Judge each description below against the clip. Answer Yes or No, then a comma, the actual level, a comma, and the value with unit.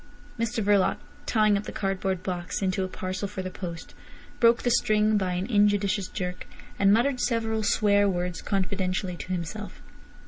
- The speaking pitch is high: Yes, high, 200 Hz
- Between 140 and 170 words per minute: Yes, average, 165 wpm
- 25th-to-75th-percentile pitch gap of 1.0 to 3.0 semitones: Yes, narrow, 2.5 semitones